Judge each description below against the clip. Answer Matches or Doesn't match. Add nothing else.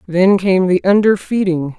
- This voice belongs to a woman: Matches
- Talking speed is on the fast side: Doesn't match